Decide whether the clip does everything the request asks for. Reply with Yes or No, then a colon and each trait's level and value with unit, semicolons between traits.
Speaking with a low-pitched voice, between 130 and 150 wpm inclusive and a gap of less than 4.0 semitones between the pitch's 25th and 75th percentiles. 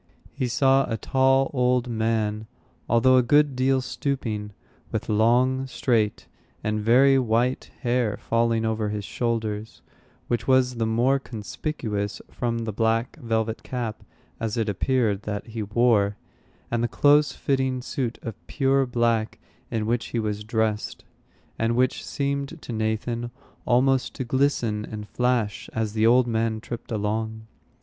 Yes: low, 115 Hz; average, 145 wpm; average, 2.7 semitones